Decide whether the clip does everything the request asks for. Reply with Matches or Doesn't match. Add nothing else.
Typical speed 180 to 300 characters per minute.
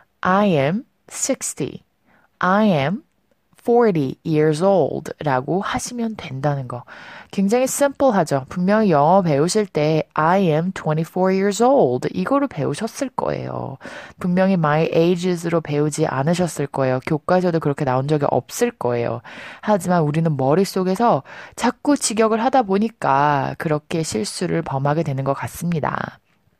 Doesn't match